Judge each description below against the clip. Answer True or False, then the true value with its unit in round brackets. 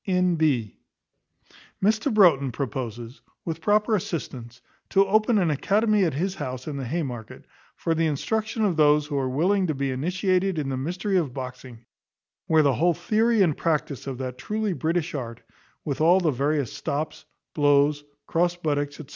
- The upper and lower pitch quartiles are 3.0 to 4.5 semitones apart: False (5.4 semitones)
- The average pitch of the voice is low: False (155 Hz)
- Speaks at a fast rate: False (165 wpm)